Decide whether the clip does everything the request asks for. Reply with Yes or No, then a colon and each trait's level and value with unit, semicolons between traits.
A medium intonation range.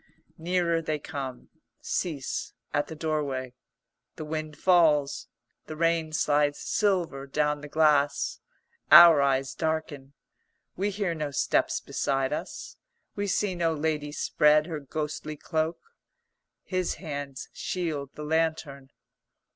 No: narrow, 2.3 semitones